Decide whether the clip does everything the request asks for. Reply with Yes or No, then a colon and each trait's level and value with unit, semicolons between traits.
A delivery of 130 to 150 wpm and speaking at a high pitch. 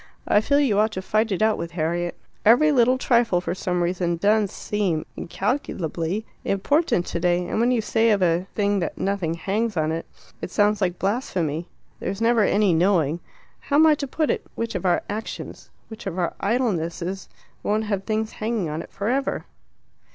No: average, 190 wpm; high, 200 Hz